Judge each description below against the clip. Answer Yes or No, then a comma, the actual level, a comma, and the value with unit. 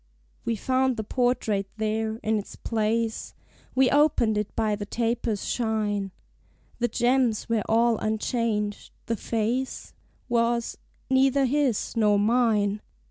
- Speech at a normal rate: No, slow, 125 wpm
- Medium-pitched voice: No, high, 225 Hz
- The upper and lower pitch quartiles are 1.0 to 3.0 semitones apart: Yes, narrow, 2.4 semitones